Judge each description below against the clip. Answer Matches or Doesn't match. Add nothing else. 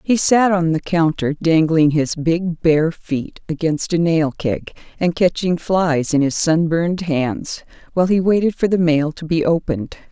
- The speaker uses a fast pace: Doesn't match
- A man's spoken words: Doesn't match